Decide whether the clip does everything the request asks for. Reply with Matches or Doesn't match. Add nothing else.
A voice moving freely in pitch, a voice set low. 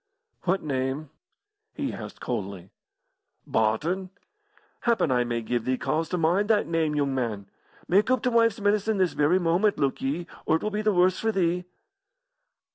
Doesn't match